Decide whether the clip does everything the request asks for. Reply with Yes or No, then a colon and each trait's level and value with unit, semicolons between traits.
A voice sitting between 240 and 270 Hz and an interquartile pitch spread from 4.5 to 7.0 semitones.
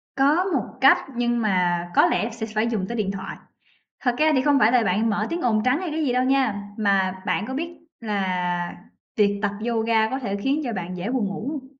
No: high, 225 Hz; average, 4.8 semitones